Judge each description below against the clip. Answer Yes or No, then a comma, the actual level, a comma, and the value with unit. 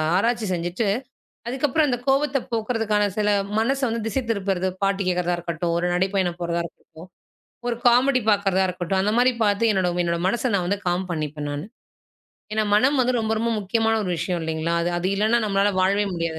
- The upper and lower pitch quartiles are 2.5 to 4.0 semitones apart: No, average, 4.7 semitones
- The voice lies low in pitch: No, high, 200 Hz